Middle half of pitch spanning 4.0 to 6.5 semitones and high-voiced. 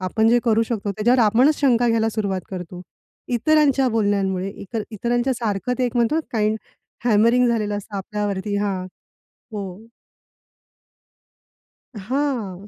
No: average, 3.2 semitones; high, 220 Hz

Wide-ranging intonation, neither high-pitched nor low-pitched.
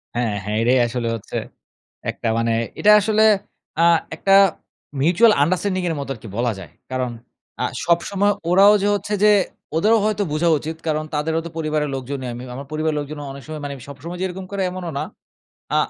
Yes: wide, 5.9 semitones; medium, 155 Hz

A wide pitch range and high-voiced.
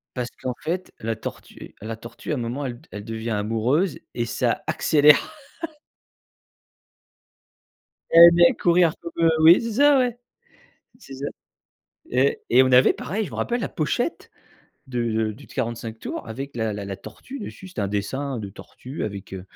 No: wide, 7.0 semitones; low, 130 Hz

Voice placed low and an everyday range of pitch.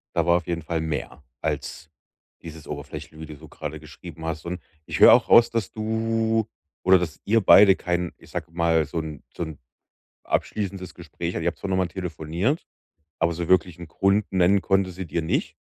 Yes: very low, 85 Hz; average, 3.2 semitones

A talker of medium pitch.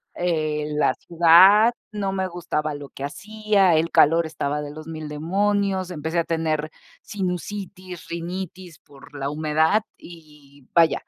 Yes: medium, 165 Hz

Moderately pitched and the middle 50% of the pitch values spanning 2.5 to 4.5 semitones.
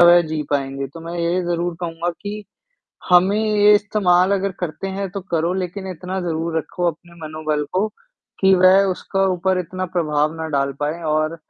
Yes: medium, 175 Hz; average, 2.9 semitones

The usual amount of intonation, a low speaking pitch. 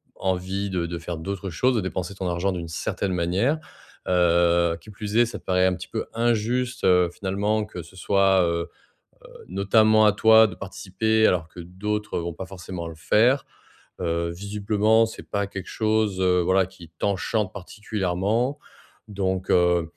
Yes: average, 3.3 semitones; very low, 95 Hz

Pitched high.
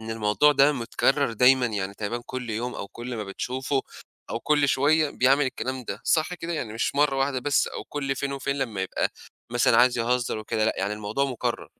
No: low, 125 Hz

